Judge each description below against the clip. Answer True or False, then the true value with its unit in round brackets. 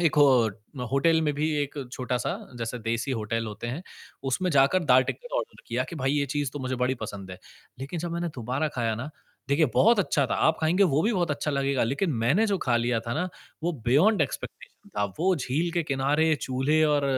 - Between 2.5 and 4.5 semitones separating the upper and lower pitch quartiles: False (4.9 semitones)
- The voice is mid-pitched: True (145 Hz)